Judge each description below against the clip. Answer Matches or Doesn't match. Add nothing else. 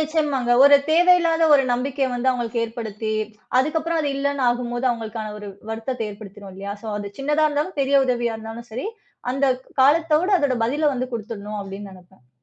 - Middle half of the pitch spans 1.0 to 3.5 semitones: Doesn't match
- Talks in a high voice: Matches